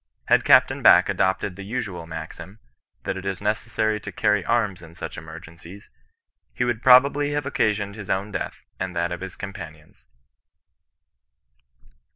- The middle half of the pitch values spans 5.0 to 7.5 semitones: No, average, 3.9 semitones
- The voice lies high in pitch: No, low, 100 Hz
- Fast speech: No, average, 150 wpm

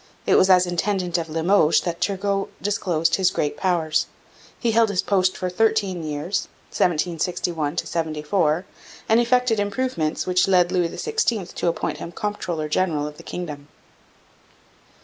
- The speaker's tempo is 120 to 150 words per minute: Yes, average, 145 wpm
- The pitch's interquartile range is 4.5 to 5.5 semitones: No, average, 3.6 semitones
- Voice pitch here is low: No, medium, 180 Hz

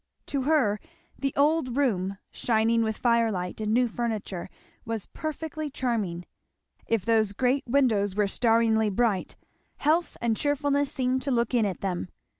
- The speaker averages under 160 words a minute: Yes, average, 145 wpm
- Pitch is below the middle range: No, high, 230 Hz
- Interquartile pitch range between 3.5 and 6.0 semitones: Yes, average, 4.4 semitones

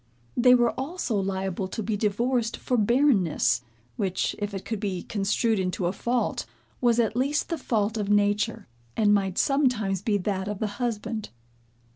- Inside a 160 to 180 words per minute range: Yes, average, 165 wpm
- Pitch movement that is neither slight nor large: Yes, average, 3.4 semitones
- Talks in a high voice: Yes, high, 210 Hz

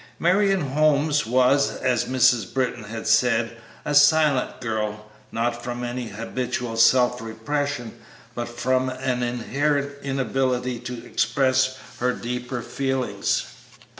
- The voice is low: Yes, low, 125 Hz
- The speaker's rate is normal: No, slow, 115 wpm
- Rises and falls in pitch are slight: Yes, narrow, 2.3 semitones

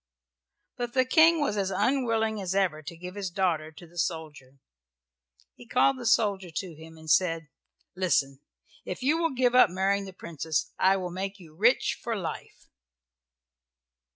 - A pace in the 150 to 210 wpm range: Yes, average, 165 wpm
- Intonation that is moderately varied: No, wide, 5.8 semitones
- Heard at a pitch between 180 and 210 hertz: Yes, high, 190 Hz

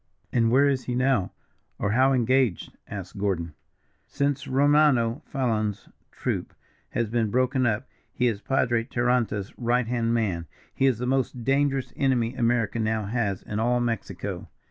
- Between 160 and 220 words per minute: No, average, 150 wpm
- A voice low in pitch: Yes, low, 120 Hz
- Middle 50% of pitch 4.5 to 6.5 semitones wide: No, average, 2.9 semitones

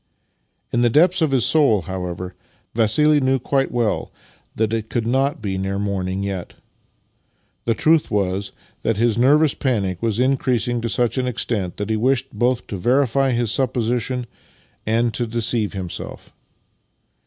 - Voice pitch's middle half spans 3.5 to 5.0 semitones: Yes, average, 4.2 semitones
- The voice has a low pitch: Yes, low, 115 Hz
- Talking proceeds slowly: No, average, 155 wpm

